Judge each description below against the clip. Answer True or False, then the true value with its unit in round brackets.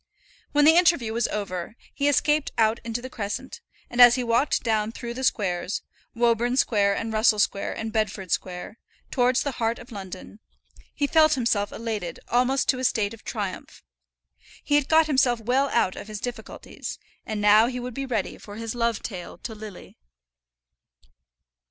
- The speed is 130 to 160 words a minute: False (175 wpm)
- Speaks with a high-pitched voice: True (230 Hz)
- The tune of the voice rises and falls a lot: False (3.2 semitones)